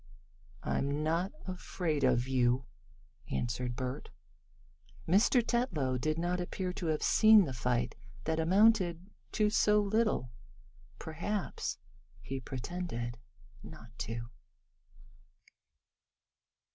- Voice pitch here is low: No, medium, 160 Hz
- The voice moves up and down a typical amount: No, wide, 7.1 semitones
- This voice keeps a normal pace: No, slow, 95 wpm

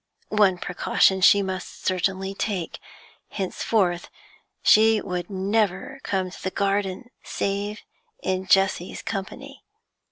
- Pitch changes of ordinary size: No, narrow, 1.7 semitones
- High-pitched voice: Yes, high, 195 Hz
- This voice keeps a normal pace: No, slow, 105 wpm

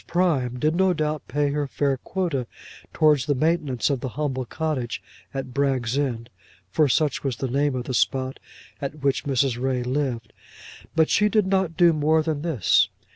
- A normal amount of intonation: Yes, average, 3.3 semitones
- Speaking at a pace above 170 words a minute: Yes, average, 180 wpm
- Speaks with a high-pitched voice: No, medium, 140 Hz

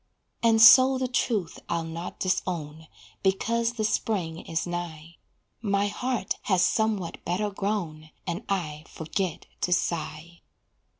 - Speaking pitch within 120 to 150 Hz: No, medium, 185 Hz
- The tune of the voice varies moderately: Yes, average, 4.7 semitones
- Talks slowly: Yes, slow, 125 wpm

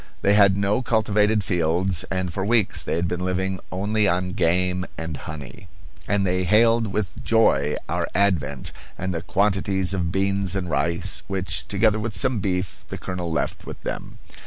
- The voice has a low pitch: Yes, very low, 95 Hz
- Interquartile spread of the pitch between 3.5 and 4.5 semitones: No, narrow, 2.5 semitones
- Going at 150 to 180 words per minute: Yes, average, 170 wpm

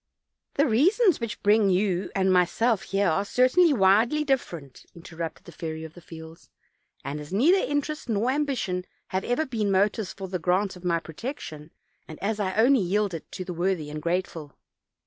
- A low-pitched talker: No, high, 195 Hz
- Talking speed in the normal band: Yes, average, 180 wpm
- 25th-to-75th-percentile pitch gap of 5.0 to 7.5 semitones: Yes, wide, 5.6 semitones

